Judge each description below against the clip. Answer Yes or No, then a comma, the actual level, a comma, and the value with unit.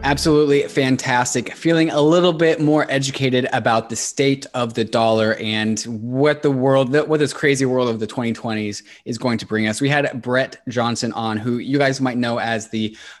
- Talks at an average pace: Yes, average, 190 wpm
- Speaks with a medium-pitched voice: No, low, 125 Hz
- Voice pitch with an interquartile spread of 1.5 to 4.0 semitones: Yes, average, 3.7 semitones